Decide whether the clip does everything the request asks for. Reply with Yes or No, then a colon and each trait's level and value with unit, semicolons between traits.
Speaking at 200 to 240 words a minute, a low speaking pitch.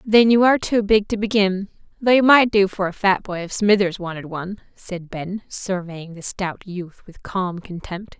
No: fast, 205 wpm; high, 195 Hz